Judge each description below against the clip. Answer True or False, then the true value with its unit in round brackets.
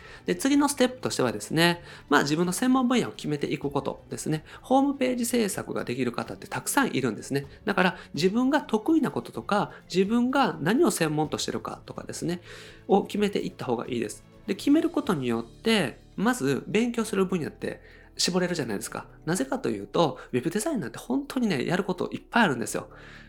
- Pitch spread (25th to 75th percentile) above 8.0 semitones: True (8.6 semitones)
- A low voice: False (195 Hz)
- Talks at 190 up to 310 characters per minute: False (430 characters per minute)